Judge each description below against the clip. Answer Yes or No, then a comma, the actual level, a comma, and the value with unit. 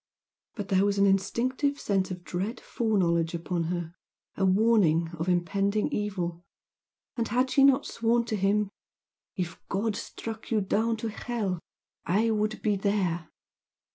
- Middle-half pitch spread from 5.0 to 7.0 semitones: No, average, 3.8 semitones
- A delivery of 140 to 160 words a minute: Yes, average, 145 wpm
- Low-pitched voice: No, high, 200 Hz